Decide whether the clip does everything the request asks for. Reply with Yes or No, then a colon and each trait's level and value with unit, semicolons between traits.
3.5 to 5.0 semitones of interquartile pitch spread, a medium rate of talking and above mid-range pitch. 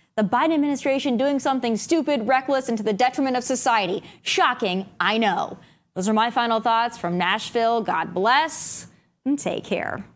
Yes: average, 3.9 semitones; average, 165 wpm; high, 240 Hz